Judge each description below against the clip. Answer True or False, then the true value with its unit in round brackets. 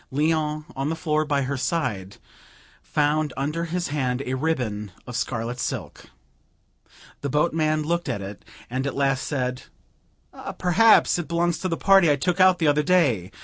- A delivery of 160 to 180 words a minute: True (165 wpm)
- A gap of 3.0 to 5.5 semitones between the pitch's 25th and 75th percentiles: True (4.4 semitones)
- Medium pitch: True (150 Hz)